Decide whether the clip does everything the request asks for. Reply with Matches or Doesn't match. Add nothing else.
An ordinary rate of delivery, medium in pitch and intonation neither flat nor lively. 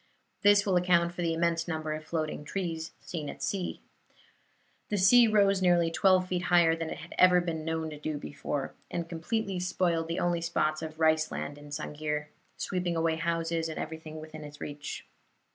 Doesn't match